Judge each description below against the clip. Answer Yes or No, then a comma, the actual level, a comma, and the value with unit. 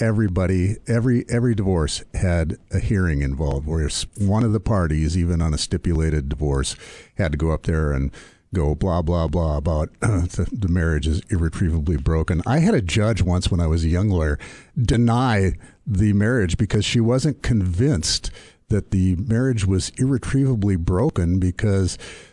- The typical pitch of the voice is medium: No, very low, 95 Hz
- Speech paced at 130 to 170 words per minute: Yes, average, 165 wpm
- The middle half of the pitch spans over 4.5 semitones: Yes, average, 5.1 semitones